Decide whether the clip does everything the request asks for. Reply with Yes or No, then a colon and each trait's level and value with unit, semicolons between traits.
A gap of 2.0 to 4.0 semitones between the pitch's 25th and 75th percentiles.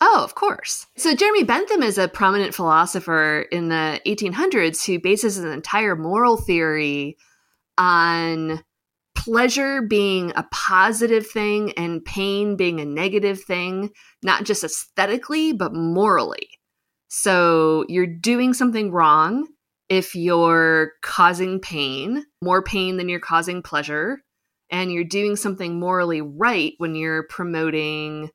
No: average, 4.6 semitones